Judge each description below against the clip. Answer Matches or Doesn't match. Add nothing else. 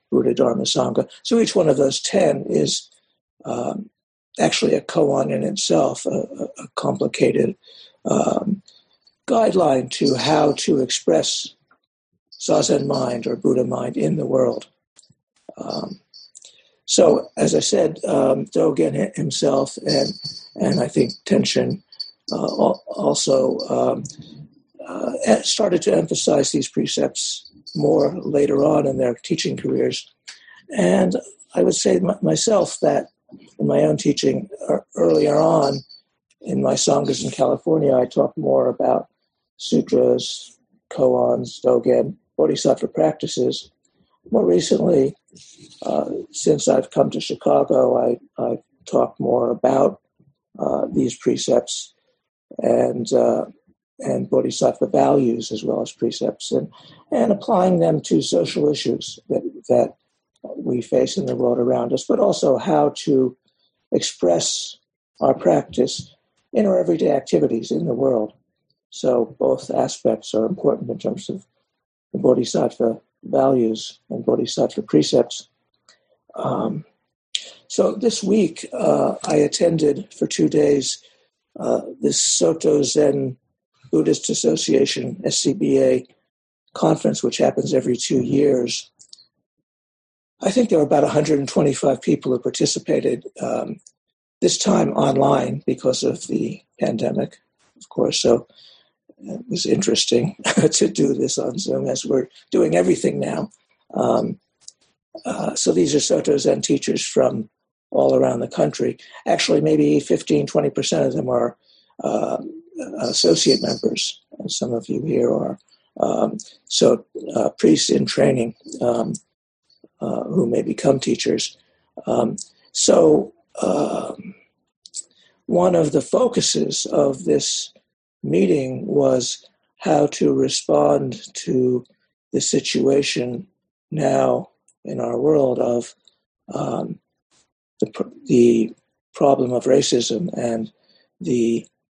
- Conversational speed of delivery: Doesn't match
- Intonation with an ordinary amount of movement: Doesn't match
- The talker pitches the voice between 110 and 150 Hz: Matches